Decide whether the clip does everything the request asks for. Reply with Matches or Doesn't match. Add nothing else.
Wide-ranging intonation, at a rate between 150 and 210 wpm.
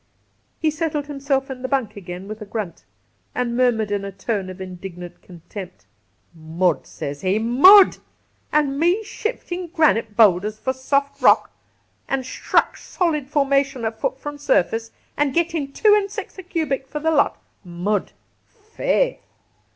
Matches